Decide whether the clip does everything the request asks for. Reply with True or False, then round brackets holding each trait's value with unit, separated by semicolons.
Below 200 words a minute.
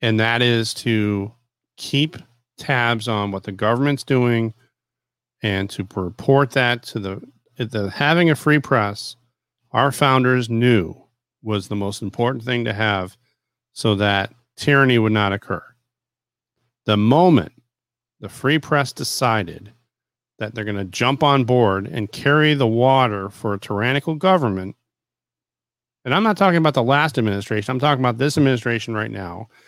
True (150 wpm)